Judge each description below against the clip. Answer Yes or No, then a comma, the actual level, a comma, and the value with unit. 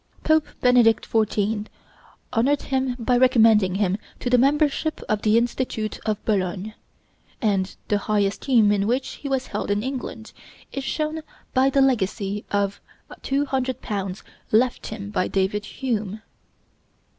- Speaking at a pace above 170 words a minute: No, slow, 135 wpm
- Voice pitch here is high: Yes, high, 225 Hz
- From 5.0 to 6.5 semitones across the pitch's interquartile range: No, average, 4.2 semitones